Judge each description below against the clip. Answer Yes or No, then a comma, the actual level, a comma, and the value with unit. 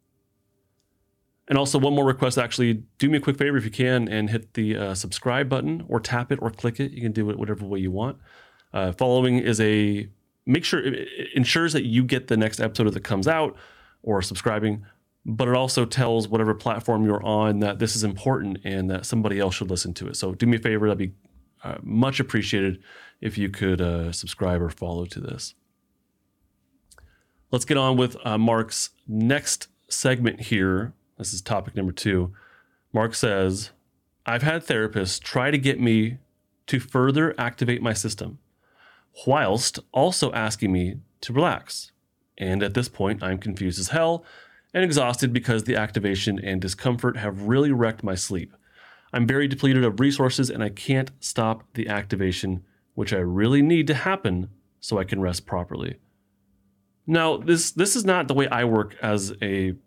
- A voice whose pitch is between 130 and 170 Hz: No, low, 110 Hz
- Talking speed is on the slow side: No, average, 180 wpm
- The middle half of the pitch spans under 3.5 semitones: No, average, 4.5 semitones